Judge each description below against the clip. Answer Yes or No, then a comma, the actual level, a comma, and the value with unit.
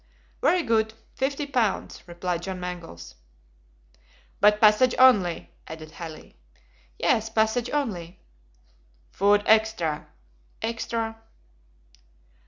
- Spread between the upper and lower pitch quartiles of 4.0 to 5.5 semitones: Yes, average, 4.5 semitones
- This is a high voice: Yes, high, 215 Hz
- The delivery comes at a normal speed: No, slow, 85 wpm